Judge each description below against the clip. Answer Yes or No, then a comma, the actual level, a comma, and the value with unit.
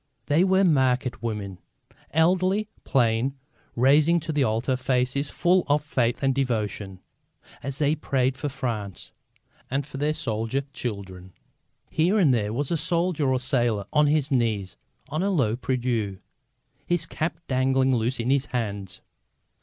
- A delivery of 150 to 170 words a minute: Yes, average, 155 wpm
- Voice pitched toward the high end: No, low, 130 Hz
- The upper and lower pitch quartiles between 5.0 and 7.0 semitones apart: No, average, 4.5 semitones